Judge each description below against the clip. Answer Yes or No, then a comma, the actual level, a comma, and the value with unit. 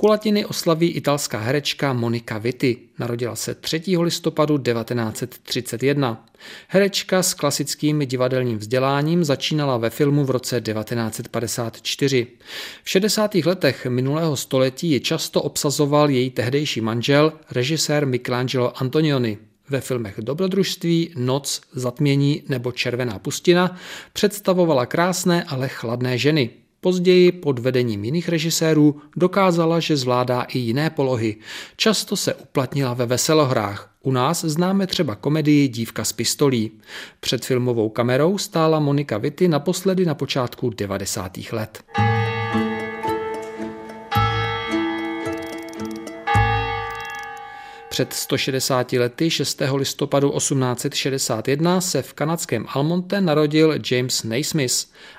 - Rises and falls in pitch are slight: No, average, 5.1 semitones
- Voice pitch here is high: No, medium, 140 Hz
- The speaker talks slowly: Yes, slow, 105 wpm